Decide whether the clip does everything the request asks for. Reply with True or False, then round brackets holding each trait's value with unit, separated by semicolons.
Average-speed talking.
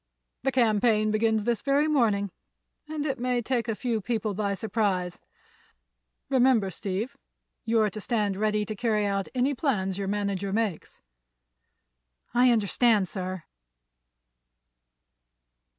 False (120 wpm)